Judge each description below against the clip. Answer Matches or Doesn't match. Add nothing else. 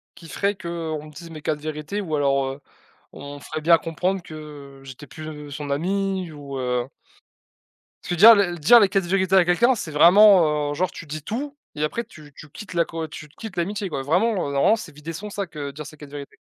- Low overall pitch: Doesn't match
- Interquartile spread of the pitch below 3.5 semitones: Doesn't match